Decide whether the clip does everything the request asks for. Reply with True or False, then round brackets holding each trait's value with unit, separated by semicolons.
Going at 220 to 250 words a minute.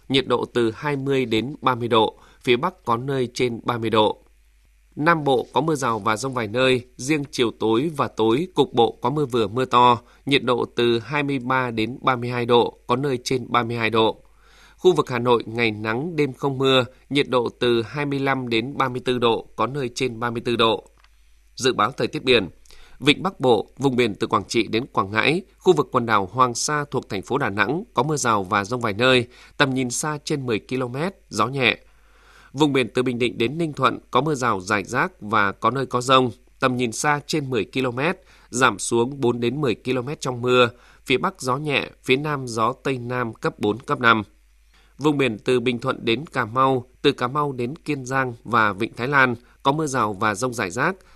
False (210 wpm)